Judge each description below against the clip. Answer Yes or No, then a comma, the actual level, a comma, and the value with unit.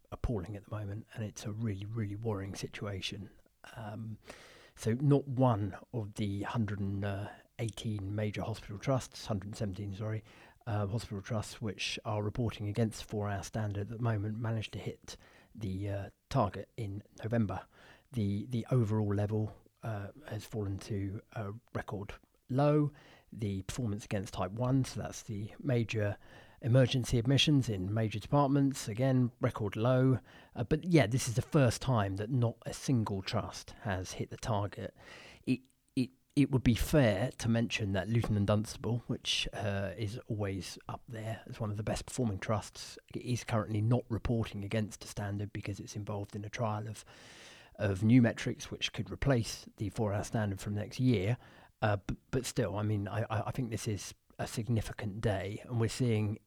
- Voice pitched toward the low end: Yes, low, 110 Hz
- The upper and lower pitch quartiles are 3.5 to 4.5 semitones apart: No, average, 2.8 semitones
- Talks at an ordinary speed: Yes, average, 170 wpm